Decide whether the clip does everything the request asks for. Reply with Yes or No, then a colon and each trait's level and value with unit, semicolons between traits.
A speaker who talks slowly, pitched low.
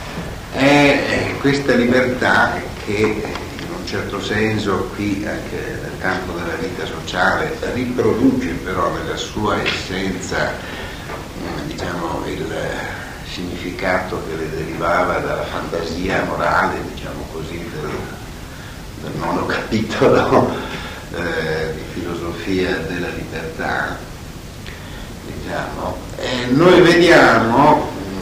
Yes: slow, 95 wpm; very low, 95 Hz